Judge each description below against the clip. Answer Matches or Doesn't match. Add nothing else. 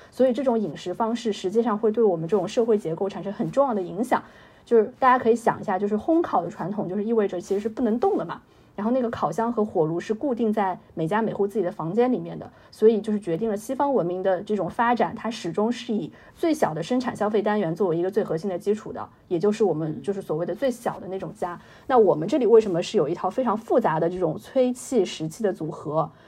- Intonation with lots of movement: Doesn't match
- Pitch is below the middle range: Doesn't match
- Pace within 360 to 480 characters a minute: Matches